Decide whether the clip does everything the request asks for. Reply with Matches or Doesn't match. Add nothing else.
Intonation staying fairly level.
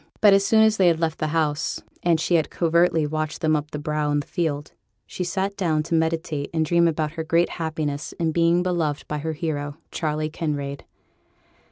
Matches